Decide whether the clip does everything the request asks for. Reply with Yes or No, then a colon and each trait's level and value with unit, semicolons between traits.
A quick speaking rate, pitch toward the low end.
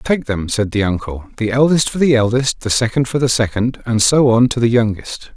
Yes: fast, 235 wpm; low, 120 Hz